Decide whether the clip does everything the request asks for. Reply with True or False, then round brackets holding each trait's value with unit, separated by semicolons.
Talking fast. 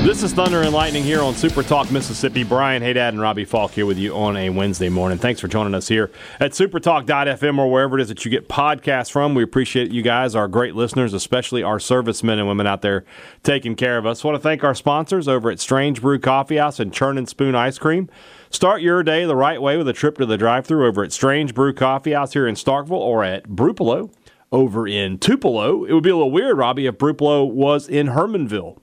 True (230 wpm)